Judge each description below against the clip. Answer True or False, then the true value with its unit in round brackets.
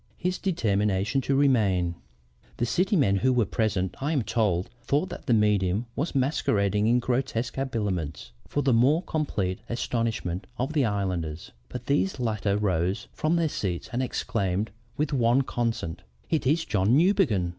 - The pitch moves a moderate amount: False (5.7 semitones)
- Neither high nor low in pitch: False (115 Hz)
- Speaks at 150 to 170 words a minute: True (155 wpm)